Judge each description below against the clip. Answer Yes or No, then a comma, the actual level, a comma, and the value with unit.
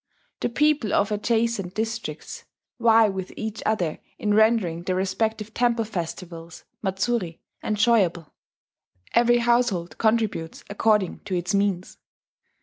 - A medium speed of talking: No, slow, 115 wpm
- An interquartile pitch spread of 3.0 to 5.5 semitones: Yes, average, 3.7 semitones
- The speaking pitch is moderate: No, high, 210 Hz